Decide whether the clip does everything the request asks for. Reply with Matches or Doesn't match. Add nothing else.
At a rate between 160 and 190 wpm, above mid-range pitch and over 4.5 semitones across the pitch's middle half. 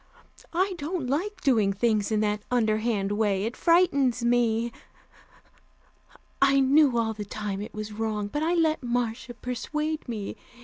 Doesn't match